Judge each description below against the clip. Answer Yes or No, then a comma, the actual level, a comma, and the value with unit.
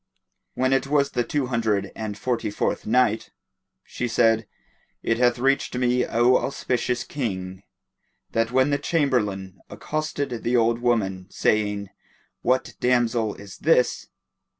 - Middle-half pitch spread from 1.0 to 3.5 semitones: Yes, average, 3.0 semitones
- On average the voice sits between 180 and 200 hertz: No, low, 120 Hz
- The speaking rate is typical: No, slow, 130 wpm